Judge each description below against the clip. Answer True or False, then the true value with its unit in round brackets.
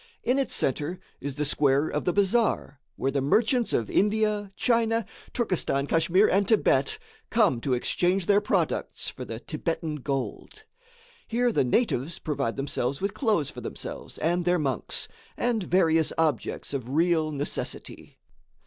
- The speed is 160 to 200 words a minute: False (150 wpm)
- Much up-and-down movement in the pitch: True (6.9 semitones)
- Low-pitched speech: False (165 Hz)